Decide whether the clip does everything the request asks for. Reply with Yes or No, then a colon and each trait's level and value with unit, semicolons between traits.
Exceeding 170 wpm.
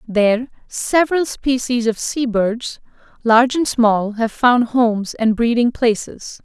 No: average, 140 wpm